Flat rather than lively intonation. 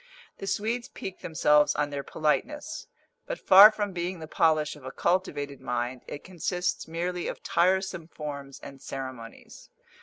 No: average, 4.8 semitones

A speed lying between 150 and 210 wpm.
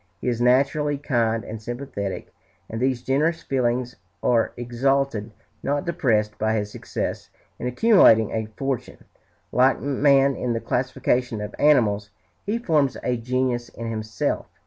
No: average, 140 wpm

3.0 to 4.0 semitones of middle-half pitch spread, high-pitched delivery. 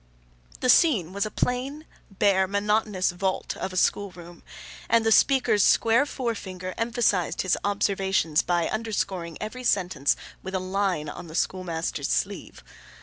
Yes: average, 3.5 semitones; high, 195 Hz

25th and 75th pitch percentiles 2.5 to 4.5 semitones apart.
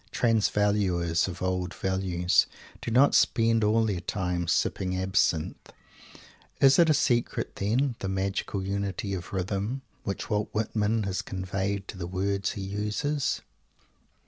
Yes: average, 2.8 semitones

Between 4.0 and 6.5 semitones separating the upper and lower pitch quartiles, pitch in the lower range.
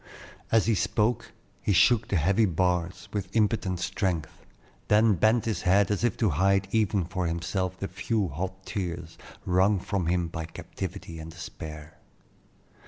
No: average, 3.3 semitones; very low, 95 Hz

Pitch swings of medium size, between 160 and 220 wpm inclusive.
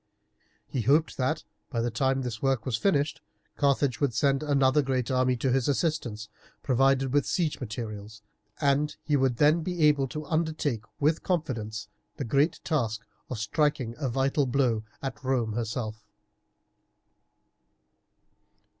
No: average, 3.8 semitones; average, 140 wpm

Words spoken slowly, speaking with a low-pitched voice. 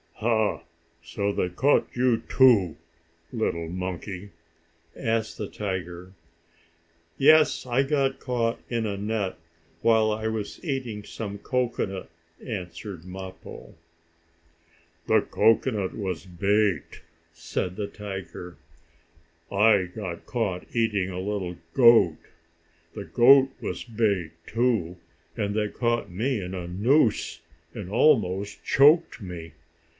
Yes: slow, 110 wpm; low, 105 Hz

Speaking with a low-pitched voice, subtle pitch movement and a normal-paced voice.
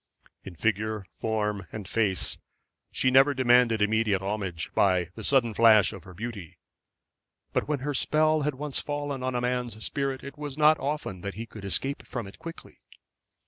No: low, 115 Hz; average, 5.2 semitones; average, 175 wpm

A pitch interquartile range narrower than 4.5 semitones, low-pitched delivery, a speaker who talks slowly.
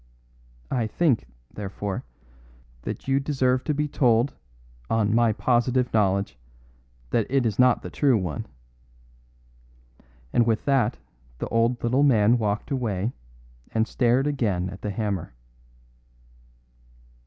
Yes: average, 3.7 semitones; low, 115 Hz; slow, 120 wpm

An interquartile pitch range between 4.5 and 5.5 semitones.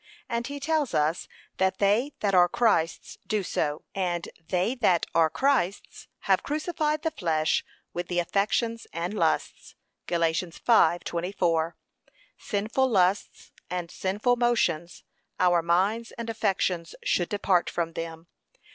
Yes: average, 5.2 semitones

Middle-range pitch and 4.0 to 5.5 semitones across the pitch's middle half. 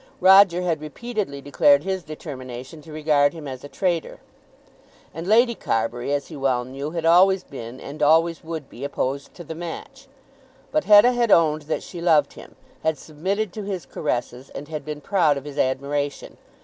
Yes: medium, 155 Hz; average, 4.5 semitones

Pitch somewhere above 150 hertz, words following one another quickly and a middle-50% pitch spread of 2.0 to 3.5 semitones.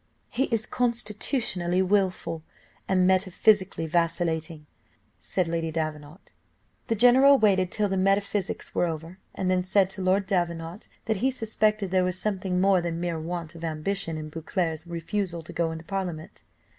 No: medium, 185 Hz; average, 155 wpm; average, 3.2 semitones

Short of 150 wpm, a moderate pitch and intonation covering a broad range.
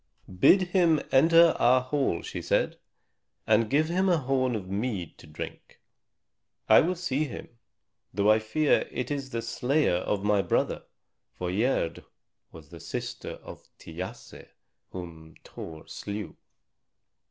No: average, 140 wpm; low, 125 Hz; wide, 7.6 semitones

